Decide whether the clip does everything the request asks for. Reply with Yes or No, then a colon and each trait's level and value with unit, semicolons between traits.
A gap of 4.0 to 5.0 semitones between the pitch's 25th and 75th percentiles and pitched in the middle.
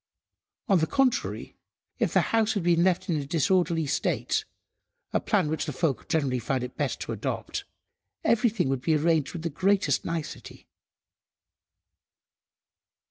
Yes: average, 4.5 semitones; medium, 165 Hz